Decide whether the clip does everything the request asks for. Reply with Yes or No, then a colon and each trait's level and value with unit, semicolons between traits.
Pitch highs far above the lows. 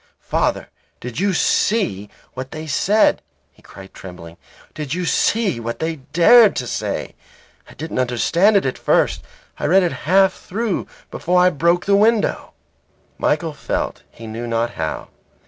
Yes: wide, 8.2 semitones